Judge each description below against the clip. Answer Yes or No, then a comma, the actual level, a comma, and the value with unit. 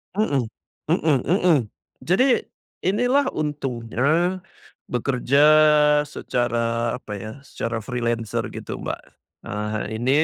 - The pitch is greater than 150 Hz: No, low, 130 Hz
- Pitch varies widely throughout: Yes, wide, 6.0 semitones